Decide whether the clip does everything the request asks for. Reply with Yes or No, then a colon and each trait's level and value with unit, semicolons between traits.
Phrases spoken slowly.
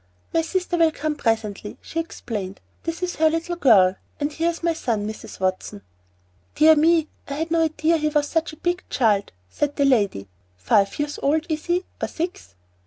No: average, 190 wpm